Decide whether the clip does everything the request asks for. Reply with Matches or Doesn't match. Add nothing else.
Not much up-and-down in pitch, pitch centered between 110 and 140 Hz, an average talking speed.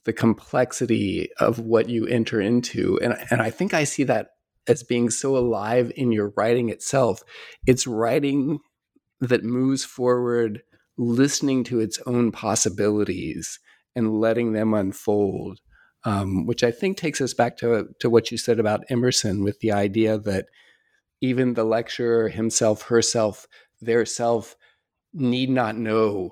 Matches